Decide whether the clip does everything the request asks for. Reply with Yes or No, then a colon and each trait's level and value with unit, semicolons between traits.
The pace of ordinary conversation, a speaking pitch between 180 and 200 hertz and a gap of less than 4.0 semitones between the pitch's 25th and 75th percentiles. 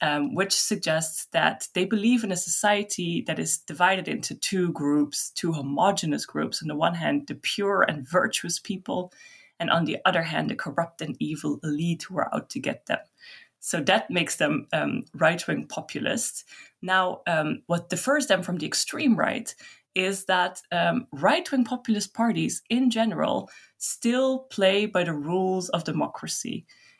No: average, 170 wpm; medium, 185 Hz; average, 4.9 semitones